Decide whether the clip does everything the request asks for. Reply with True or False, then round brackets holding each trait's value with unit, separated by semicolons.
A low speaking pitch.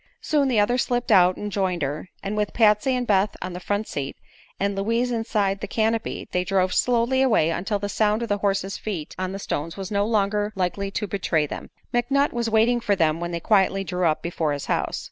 False (200 Hz)